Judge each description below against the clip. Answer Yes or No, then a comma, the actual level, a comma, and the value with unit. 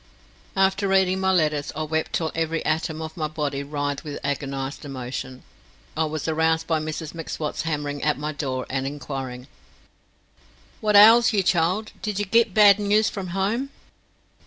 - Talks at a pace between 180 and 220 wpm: No, average, 160 wpm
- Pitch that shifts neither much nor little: Yes, average, 5.0 semitones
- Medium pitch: Yes, medium, 160 Hz